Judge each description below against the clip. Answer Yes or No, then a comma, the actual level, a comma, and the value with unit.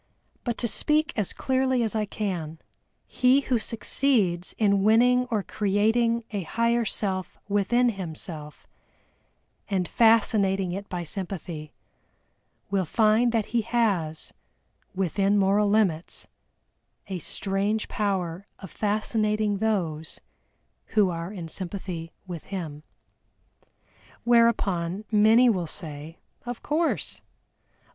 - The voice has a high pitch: Yes, high, 205 Hz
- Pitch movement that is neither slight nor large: Yes, average, 4.1 semitones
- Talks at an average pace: No, slow, 110 wpm